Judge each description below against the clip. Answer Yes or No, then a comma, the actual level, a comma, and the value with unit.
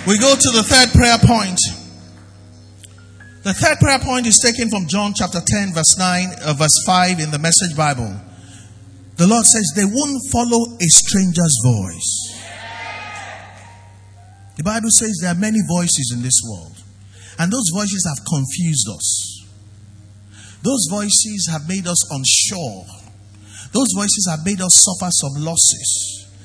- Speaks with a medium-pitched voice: Yes, medium, 155 Hz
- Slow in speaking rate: No, average, 145 wpm